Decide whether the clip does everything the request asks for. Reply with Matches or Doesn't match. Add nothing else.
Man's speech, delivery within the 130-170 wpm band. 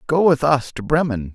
Doesn't match